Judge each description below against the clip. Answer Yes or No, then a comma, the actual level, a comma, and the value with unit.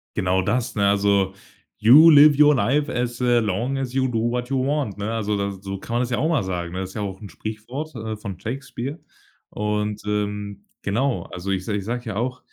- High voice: No, low, 110 Hz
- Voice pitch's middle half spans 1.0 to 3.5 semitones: No, average, 4.1 semitones